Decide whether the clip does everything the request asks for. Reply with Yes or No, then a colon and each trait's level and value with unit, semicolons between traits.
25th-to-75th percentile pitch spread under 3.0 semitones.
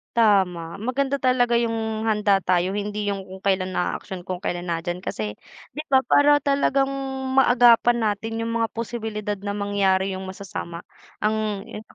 No: average, 3.6 semitones